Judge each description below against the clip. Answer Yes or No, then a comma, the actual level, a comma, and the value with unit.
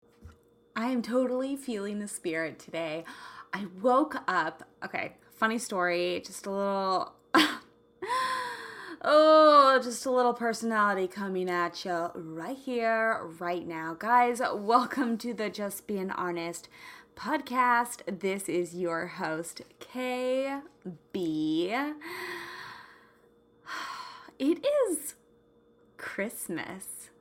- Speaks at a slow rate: Yes, slow, 95 wpm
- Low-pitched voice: No, high, 225 Hz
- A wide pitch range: Yes, wide, 7.4 semitones